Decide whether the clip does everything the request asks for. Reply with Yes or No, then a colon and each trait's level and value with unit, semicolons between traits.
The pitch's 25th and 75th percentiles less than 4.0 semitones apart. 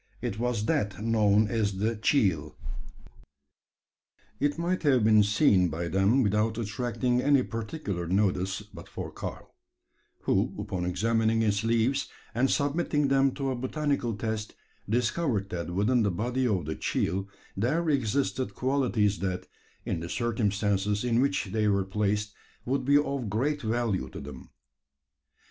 No: average, 4.5 semitones